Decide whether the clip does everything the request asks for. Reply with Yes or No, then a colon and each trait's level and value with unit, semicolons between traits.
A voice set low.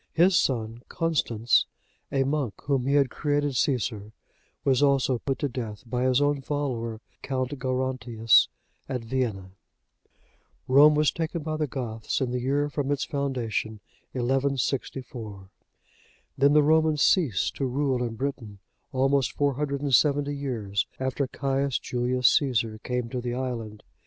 Yes: low, 130 Hz